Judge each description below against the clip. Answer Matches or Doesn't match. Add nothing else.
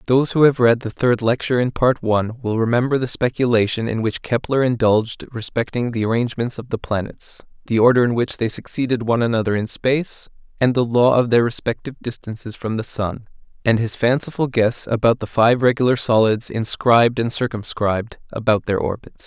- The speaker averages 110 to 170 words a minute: Doesn't match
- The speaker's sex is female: Doesn't match